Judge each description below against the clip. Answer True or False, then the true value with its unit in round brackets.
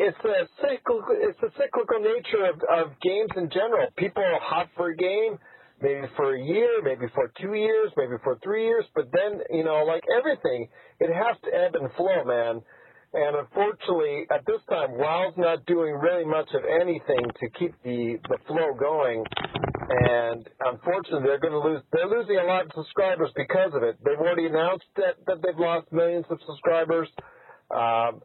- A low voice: False (185 Hz)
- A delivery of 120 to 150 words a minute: False (185 wpm)